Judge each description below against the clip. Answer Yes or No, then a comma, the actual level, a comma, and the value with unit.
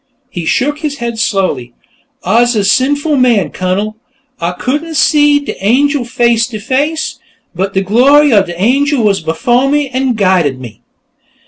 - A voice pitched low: No, high, 235 Hz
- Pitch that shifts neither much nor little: No, wide, 6.5 semitones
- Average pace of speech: Yes, average, 155 wpm